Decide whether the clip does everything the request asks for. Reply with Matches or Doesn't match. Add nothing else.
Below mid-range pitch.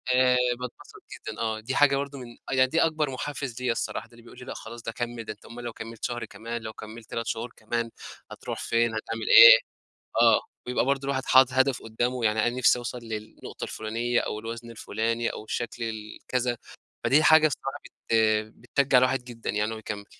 Matches